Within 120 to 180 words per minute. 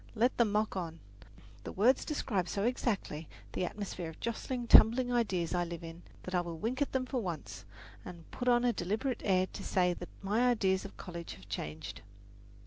No: average, 195 wpm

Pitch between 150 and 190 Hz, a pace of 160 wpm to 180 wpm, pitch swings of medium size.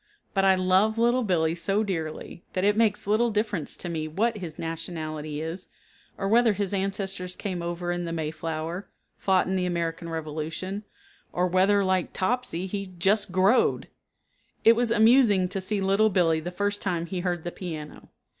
Yes: medium, 185 Hz; average, 175 wpm; average, 3.3 semitones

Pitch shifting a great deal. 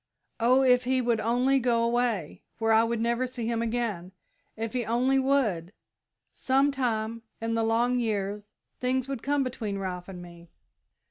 No: narrow, 2.6 semitones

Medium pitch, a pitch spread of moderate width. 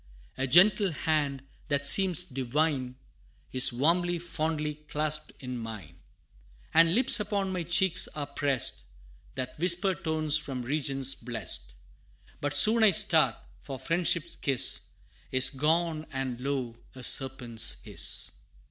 Yes: medium, 150 Hz; average, 4.5 semitones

